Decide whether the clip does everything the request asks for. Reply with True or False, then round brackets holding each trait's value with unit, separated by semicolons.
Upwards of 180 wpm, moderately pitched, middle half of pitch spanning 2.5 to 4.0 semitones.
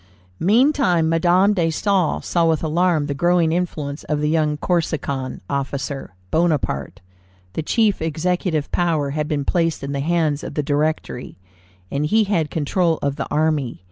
False (155 wpm; 160 Hz; 3.1 semitones)